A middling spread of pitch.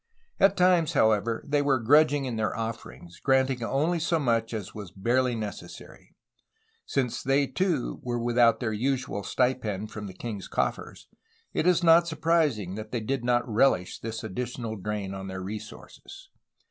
Yes: average, 4.6 semitones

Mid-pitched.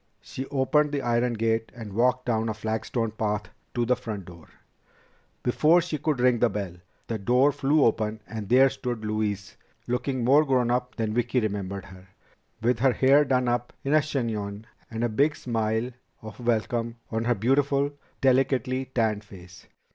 No: low, 120 Hz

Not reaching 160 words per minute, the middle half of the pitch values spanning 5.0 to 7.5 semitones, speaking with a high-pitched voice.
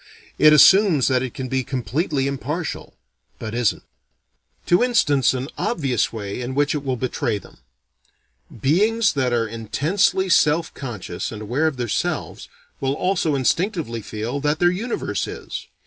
No: average, 150 wpm; average, 5.3 semitones; medium, 140 Hz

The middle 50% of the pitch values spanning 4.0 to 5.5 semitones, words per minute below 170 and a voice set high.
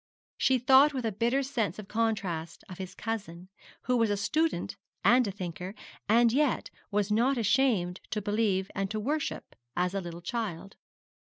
No: average, 4.4 semitones; average, 175 wpm; high, 215 Hz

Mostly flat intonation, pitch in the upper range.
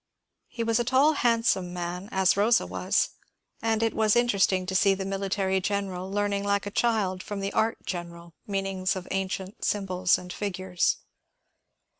Yes: narrow, 2.2 semitones; high, 195 Hz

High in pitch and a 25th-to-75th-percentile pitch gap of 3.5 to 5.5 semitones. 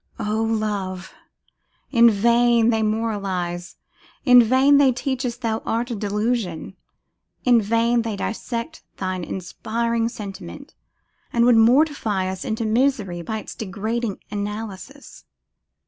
No: high, 225 Hz; average, 2.9 semitones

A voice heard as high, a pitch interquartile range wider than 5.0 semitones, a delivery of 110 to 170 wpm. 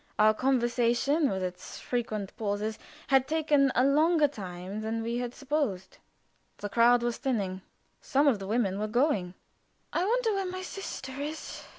Yes: high, 240 Hz; wide, 5.5 semitones; average, 160 wpm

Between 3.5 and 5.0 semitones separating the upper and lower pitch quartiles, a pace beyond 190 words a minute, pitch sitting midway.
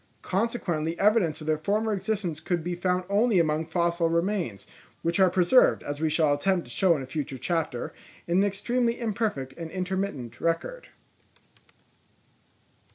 No: average, 4.1 semitones; average, 155 wpm; medium, 175 Hz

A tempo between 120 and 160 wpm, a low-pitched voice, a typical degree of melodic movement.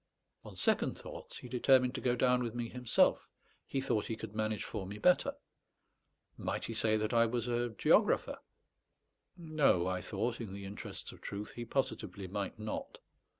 No: average, 175 wpm; low, 115 Hz; average, 3.0 semitones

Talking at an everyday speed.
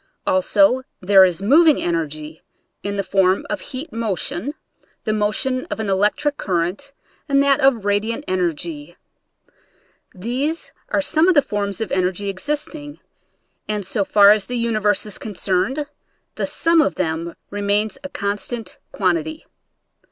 Yes: average, 145 wpm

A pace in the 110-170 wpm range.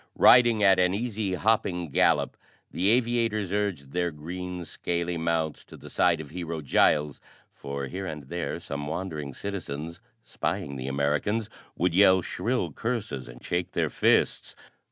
Yes: average, 150 wpm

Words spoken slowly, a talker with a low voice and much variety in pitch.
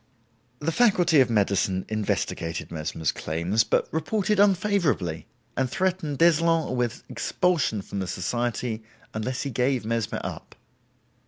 Yes: slow, 120 wpm; low, 125 Hz; wide, 8.6 semitones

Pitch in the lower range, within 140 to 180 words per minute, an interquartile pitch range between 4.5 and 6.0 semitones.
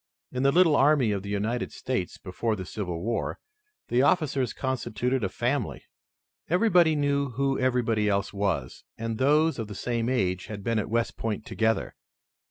Yes: low, 120 Hz; average, 170 wpm; average, 4.9 semitones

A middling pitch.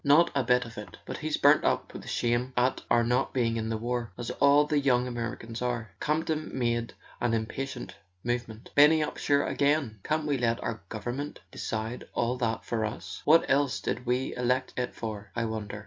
No: low, 120 Hz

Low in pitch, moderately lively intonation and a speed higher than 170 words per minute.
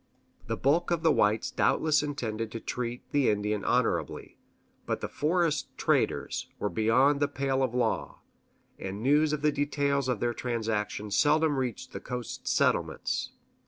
No: low, 130 Hz; average, 4.5 semitones; average, 155 wpm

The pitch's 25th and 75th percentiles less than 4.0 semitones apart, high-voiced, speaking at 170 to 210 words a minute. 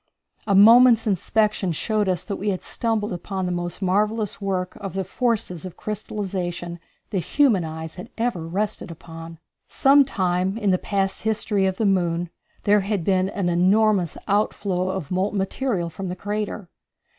No: average, 2.9 semitones; high, 195 Hz; average, 160 wpm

